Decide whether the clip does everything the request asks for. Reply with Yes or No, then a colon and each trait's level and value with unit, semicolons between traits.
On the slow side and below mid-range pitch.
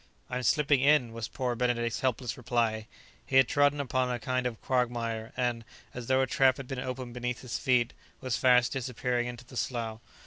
No: average, 195 wpm; low, 125 Hz